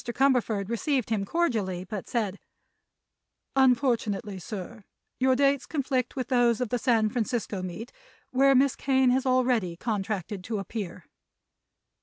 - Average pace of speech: No, slow, 130 wpm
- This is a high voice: Yes, high, 235 Hz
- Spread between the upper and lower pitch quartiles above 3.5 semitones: Yes, average, 4.2 semitones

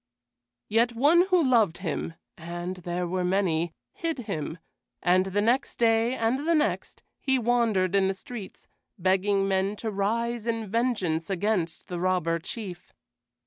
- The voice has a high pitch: Yes, high, 200 Hz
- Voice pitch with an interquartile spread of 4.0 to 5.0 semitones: Yes, average, 4.6 semitones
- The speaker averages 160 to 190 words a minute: No, average, 145 wpm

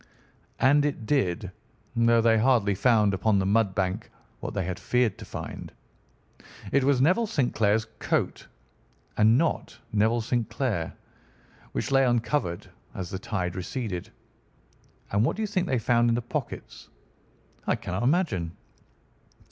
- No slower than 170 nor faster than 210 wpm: No, average, 150 wpm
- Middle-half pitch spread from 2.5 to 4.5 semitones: No, average, 4.9 semitones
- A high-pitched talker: No, low, 115 Hz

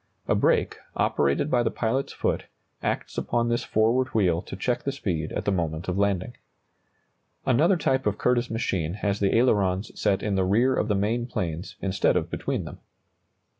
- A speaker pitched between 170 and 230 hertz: No, low, 105 Hz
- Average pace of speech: Yes, average, 180 wpm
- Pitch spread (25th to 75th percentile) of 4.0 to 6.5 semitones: Yes, average, 4.5 semitones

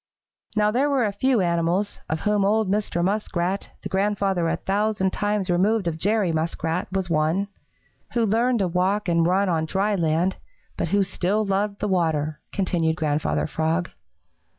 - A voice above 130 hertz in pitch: Yes, high, 190 Hz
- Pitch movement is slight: No, average, 3.7 semitones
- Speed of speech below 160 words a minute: No, average, 165 wpm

